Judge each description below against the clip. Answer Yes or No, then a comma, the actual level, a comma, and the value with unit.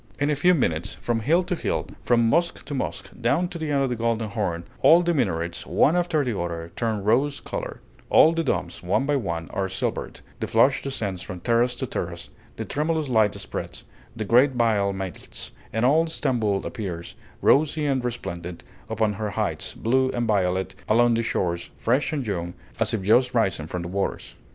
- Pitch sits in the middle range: No, low, 115 Hz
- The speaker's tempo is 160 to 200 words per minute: Yes, average, 195 wpm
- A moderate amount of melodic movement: No, wide, 6.4 semitones